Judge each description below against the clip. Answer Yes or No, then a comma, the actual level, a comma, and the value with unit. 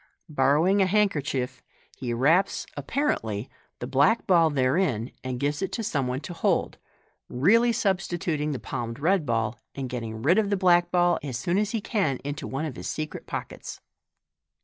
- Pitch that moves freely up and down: Yes, wide, 6.7 semitones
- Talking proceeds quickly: No, average, 170 wpm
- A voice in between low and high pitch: Yes, medium, 150 Hz